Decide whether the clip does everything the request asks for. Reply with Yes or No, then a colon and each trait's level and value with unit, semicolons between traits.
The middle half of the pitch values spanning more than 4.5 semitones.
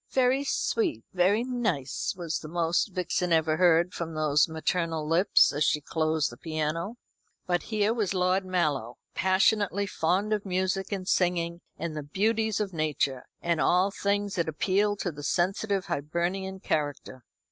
No: average, 3.9 semitones